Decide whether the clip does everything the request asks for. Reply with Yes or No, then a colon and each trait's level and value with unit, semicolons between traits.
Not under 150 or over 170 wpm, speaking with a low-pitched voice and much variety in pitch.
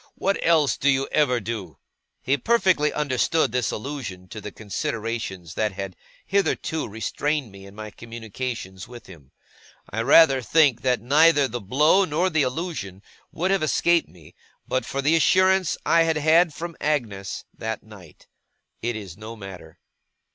Yes: average, 155 wpm; low, 125 Hz; wide, 6.8 semitones